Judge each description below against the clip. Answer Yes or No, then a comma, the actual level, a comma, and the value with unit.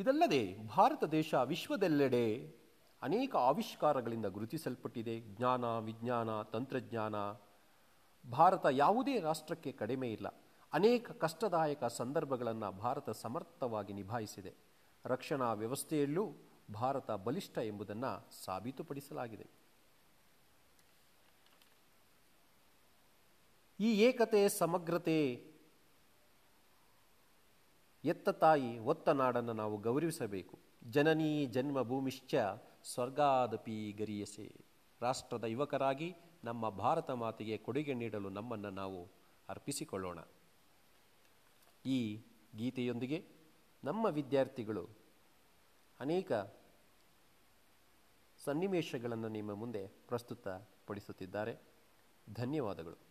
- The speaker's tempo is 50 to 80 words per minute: Yes, average, 70 wpm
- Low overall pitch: Yes, low, 125 Hz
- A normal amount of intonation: No, wide, 6.1 semitones